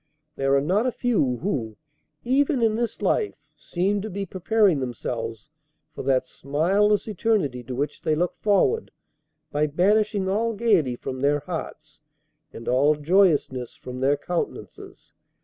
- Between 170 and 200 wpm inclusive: No, average, 145 wpm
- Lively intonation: Yes, wide, 7.5 semitones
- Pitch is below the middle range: No, medium, 175 Hz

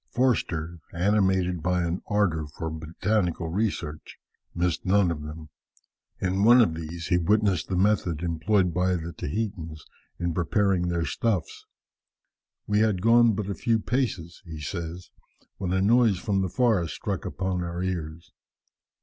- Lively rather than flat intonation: No, average, 3.6 semitones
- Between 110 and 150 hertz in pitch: No, very low, 90 Hz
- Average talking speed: Yes, average, 150 wpm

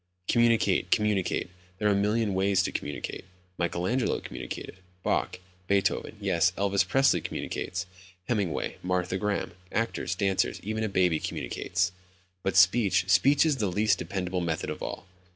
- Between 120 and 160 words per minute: Yes, average, 145 wpm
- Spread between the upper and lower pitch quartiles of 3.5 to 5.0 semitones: No, average, 2.7 semitones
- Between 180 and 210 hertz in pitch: No, very low, 95 Hz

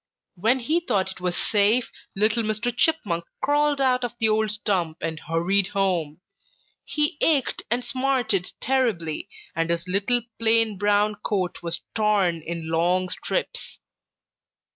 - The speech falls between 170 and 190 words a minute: No, average, 140 wpm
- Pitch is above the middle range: Yes, high, 210 Hz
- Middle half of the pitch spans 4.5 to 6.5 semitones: Yes, average, 5.2 semitones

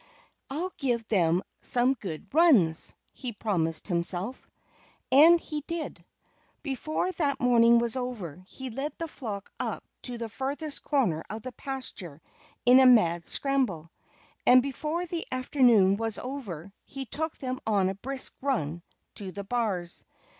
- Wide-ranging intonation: Yes, wide, 6.0 semitones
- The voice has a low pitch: No, high, 245 Hz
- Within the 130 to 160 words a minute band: Yes, average, 145 wpm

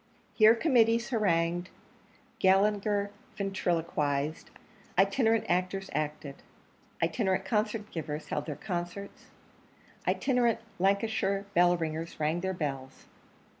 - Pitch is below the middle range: No, high, 190 Hz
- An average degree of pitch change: Yes, average, 4.1 semitones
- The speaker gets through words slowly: Yes, slow, 95 wpm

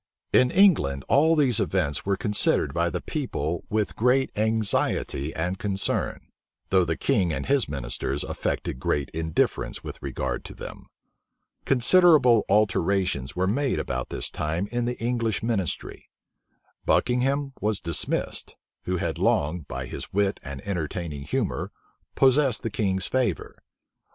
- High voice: No, low, 100 Hz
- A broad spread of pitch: Yes, wide, 7.3 semitones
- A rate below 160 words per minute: Yes, slow, 135 wpm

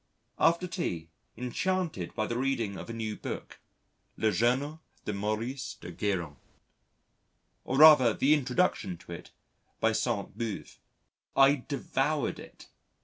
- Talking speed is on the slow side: Yes, slow, 130 wpm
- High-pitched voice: No, low, 120 Hz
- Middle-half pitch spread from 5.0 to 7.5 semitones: Yes, wide, 5.4 semitones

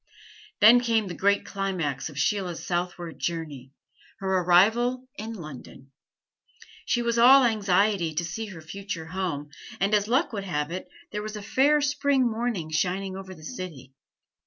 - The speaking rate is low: No, average, 160 wpm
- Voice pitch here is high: Yes, high, 195 Hz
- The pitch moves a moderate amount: Yes, average, 5.0 semitones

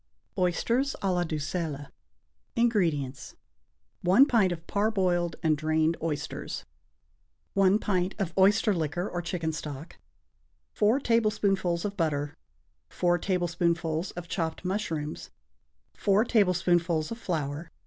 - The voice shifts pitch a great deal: No, average, 3.7 semitones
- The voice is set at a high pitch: No, medium, 175 Hz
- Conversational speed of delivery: No, slow, 110 wpm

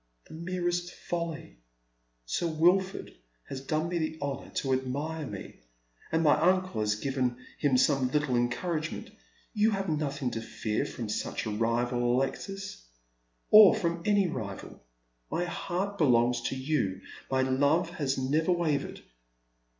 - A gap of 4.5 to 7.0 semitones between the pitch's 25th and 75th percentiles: Yes, wide, 5.6 semitones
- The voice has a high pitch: No, medium, 145 Hz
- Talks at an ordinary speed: Yes, average, 145 wpm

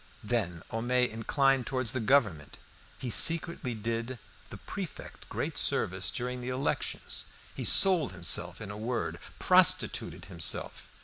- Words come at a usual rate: No, slow, 130 wpm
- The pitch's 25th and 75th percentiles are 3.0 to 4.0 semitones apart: Yes, average, 3.7 semitones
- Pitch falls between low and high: No, low, 120 Hz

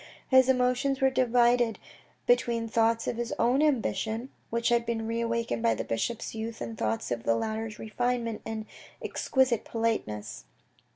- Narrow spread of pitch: Yes, narrow, 1.9 semitones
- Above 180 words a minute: No, average, 155 wpm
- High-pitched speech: Yes, high, 230 Hz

